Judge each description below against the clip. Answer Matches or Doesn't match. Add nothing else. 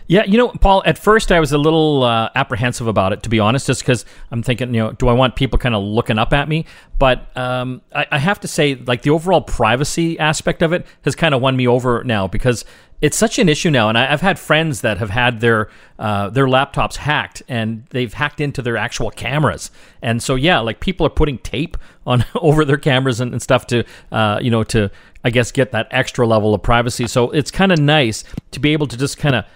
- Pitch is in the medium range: Doesn't match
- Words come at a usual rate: Doesn't match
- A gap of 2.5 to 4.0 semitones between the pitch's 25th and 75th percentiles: Doesn't match